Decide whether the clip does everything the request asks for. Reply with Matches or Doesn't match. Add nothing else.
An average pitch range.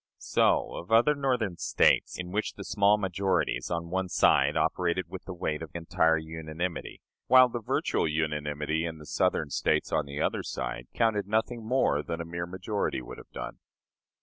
Matches